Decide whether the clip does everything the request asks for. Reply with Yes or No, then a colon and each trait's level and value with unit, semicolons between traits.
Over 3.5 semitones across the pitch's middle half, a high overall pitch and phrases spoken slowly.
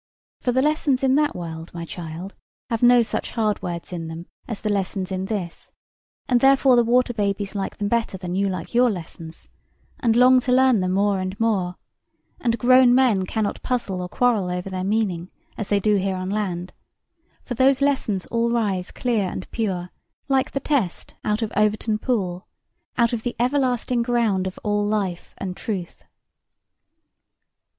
No: average, 4.6 semitones; high, 210 Hz; average, 175 wpm